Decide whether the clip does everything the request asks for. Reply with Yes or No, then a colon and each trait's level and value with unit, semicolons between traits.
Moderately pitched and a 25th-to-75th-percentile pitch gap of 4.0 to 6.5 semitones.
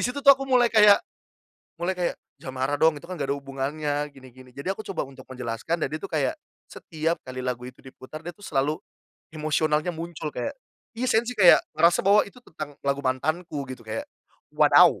Yes: medium, 155 Hz; average, 4.8 semitones